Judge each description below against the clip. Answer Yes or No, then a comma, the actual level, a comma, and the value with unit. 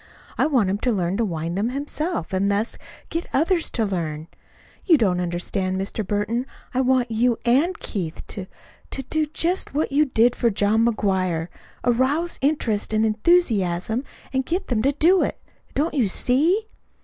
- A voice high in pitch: Yes, high, 235 Hz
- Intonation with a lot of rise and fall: Yes, wide, 6.6 semitones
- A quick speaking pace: No, average, 175 wpm